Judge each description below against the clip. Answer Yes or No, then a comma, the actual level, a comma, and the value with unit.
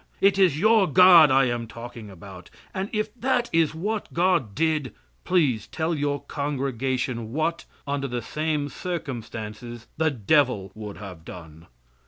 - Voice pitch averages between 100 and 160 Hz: Yes, medium, 140 Hz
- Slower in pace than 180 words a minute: Yes, average, 145 wpm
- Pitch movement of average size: No, wide, 6.2 semitones